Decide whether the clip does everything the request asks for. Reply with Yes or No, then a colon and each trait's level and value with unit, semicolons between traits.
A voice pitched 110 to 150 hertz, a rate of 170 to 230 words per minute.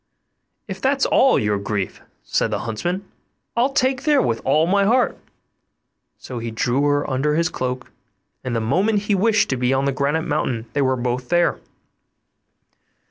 Yes: medium, 140 Hz; average, 175 wpm